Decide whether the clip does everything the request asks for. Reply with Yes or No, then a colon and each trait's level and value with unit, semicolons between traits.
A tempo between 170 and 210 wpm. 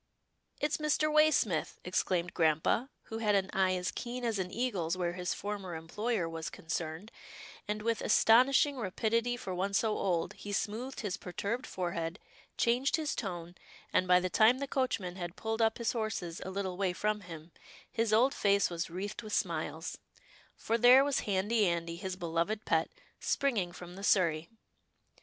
Yes: average, 175 wpm